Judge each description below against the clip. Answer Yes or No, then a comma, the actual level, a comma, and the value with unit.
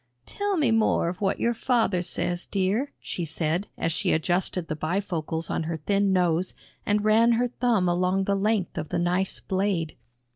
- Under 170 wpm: No, average, 180 wpm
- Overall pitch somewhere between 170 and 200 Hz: Yes, high, 190 Hz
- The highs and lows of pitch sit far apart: No, average, 3.7 semitones